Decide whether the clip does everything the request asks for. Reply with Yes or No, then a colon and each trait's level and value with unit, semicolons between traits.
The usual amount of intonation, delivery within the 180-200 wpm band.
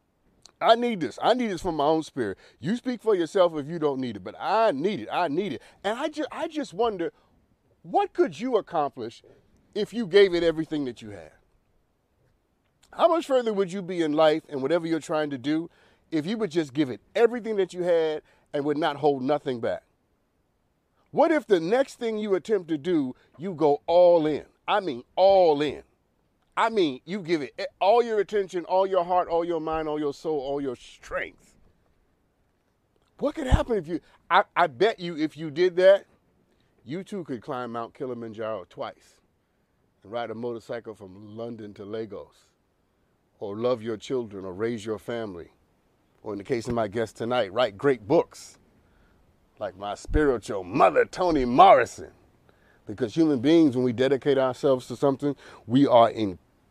No: wide, 7.6 semitones; average, 185 wpm